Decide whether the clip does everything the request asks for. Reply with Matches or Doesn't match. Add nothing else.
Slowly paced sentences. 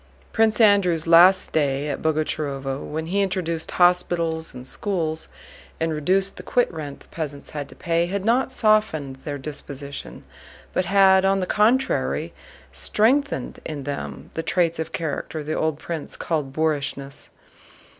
Doesn't match